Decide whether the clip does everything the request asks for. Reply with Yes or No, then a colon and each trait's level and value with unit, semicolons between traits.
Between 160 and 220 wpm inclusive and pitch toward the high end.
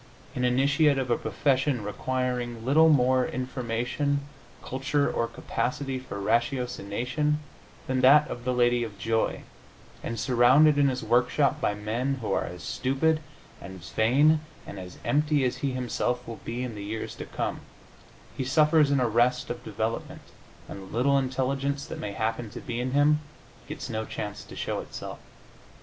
No: average, 165 wpm; low, 125 Hz